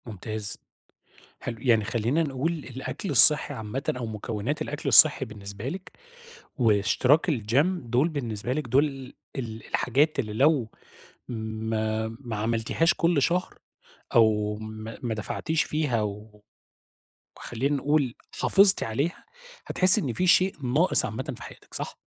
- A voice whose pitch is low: Yes, low, 125 Hz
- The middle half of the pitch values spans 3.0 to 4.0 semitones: No, wide, 5.5 semitones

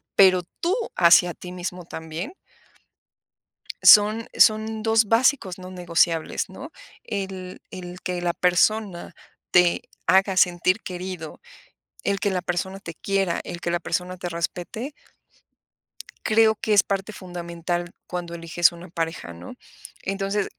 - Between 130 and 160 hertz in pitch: No, medium, 180 Hz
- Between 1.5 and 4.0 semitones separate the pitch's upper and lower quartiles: Yes, narrow, 2.4 semitones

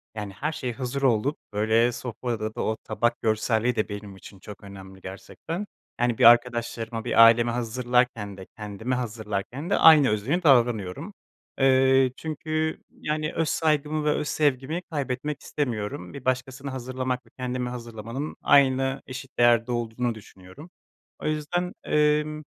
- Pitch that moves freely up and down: No, average, 4.2 semitones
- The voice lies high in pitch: No, low, 125 Hz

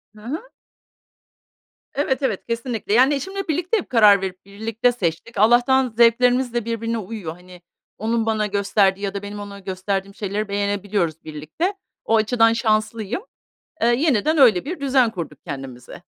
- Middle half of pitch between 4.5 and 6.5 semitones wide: No, average, 3.7 semitones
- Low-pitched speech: No, high, 220 Hz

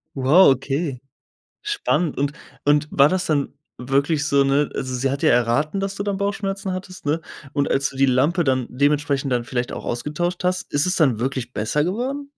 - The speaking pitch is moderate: Yes, medium, 145 Hz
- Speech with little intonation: No, average, 5.1 semitones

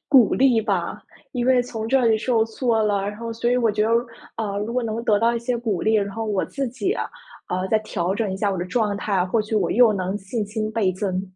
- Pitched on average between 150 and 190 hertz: No, high, 220 Hz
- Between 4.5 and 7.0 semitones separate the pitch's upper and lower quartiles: No, average, 2.8 semitones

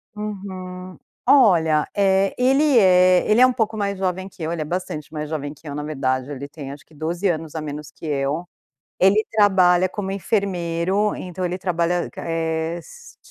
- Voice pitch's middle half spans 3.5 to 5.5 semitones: Yes, average, 3.8 semitones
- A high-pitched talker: No, medium, 180 Hz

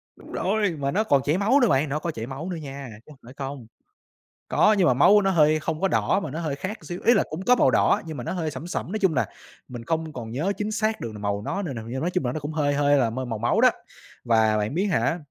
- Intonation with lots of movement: Yes, wide, 6.2 semitones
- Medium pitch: Yes, medium, 155 Hz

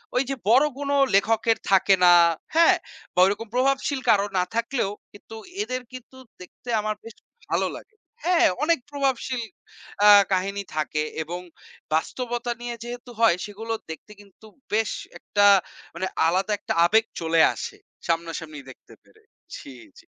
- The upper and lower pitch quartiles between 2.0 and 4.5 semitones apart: No, average, 5.2 semitones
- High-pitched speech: Yes, high, 220 Hz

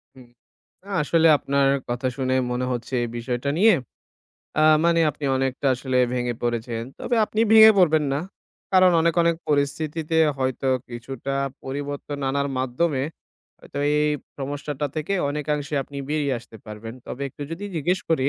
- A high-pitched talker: No, medium, 140 Hz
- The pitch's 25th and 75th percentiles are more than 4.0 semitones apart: No, average, 3.4 semitones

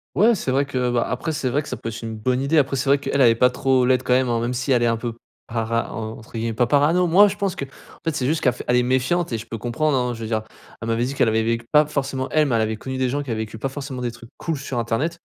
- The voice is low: Yes, low, 125 Hz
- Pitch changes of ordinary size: Yes, average, 3.4 semitones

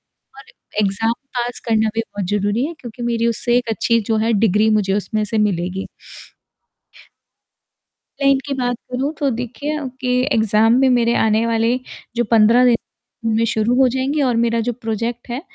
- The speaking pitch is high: Yes, high, 230 Hz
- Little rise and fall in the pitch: Yes, narrow, 2.3 semitones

